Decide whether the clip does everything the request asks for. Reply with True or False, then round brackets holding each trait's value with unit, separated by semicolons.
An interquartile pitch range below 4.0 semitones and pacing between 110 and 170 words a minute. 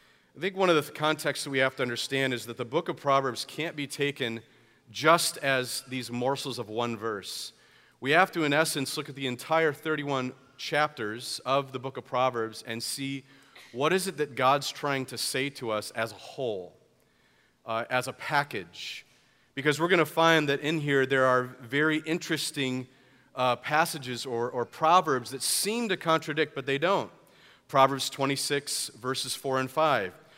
False (3.1 semitones; 180 wpm)